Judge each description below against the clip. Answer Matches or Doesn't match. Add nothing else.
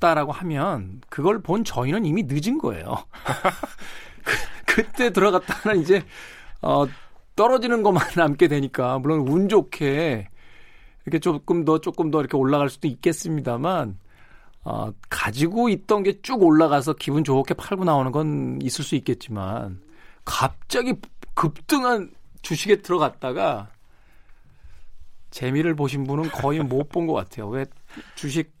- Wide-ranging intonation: Doesn't match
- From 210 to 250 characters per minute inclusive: Doesn't match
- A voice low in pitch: Doesn't match